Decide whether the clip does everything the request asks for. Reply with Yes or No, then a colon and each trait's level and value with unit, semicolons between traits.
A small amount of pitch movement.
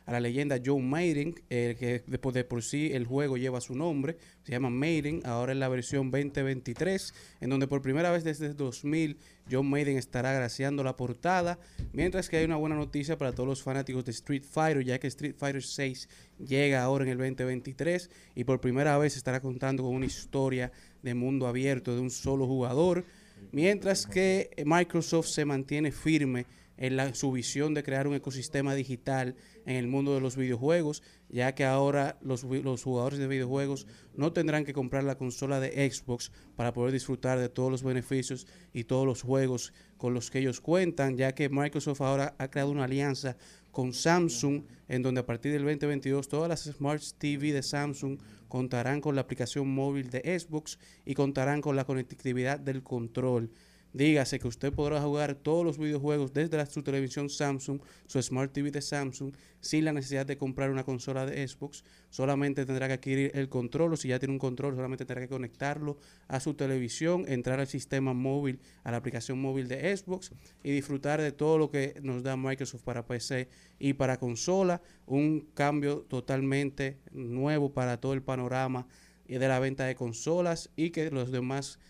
Yes: narrow, 2.2 semitones